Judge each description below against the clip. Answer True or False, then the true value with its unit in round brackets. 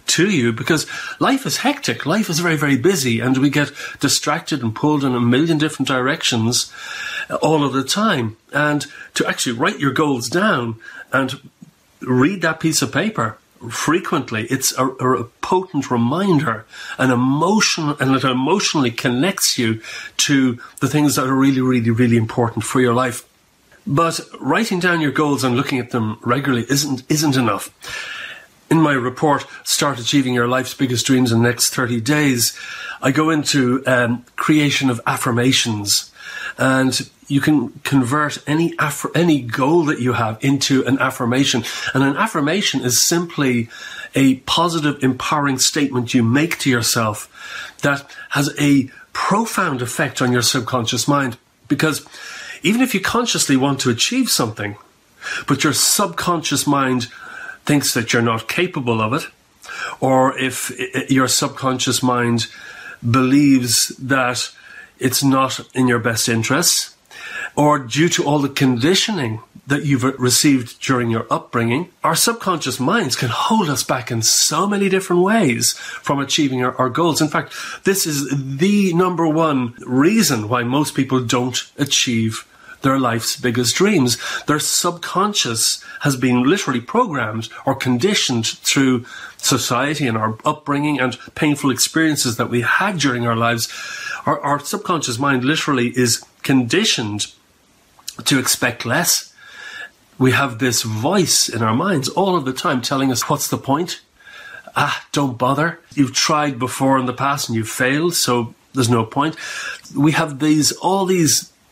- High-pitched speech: False (135 Hz)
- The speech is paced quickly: False (150 wpm)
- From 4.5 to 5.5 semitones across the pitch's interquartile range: False (3.4 semitones)